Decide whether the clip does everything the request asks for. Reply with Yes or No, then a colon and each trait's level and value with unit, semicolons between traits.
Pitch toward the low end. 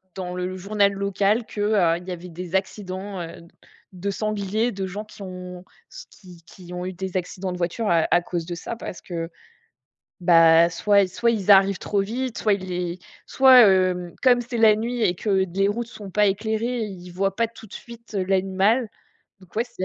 No: high, 195 Hz